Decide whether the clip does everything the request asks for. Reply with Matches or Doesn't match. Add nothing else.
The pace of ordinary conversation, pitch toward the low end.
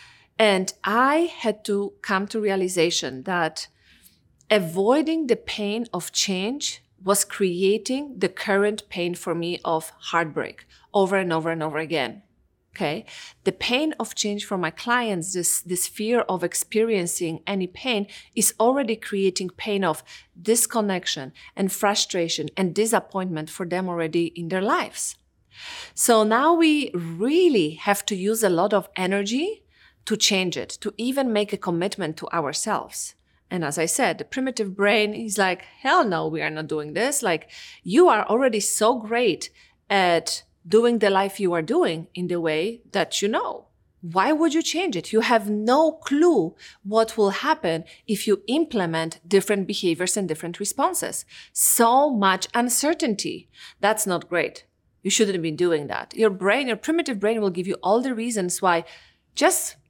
Doesn't match